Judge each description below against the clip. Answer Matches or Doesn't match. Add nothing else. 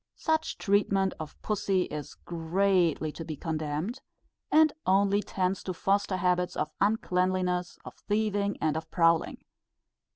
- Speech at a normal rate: Doesn't match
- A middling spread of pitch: Matches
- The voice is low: Doesn't match